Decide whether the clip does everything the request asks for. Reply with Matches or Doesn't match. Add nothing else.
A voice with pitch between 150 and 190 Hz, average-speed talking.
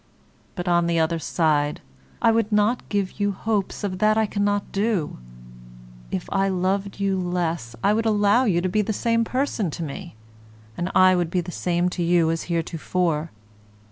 Matches